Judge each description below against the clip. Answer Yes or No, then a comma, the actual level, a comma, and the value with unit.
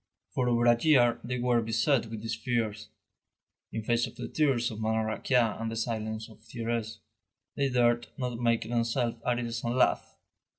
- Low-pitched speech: Yes, low, 115 Hz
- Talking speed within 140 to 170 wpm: No, average, 180 wpm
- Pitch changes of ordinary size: No, narrow, 1.5 semitones